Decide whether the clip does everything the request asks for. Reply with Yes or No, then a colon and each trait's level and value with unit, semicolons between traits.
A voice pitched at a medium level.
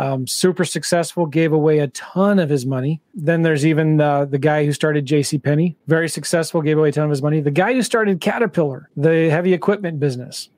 Yes: medium, 160 Hz